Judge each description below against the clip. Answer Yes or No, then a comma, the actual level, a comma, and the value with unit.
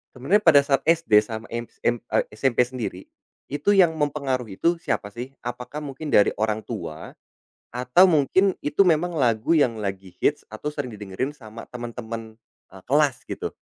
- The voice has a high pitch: No, low, 125 Hz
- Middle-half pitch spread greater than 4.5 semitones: Yes, average, 5.1 semitones